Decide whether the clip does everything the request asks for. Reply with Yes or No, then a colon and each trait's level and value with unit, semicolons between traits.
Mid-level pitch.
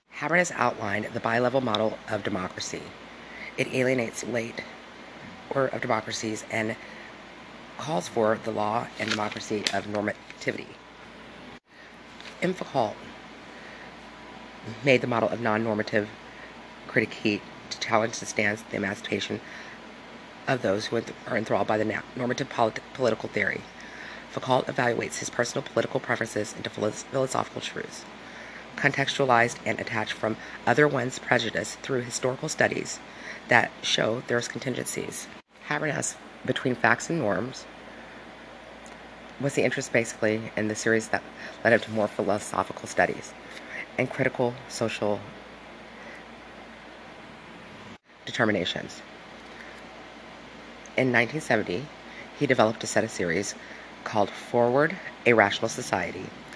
No: low, 115 Hz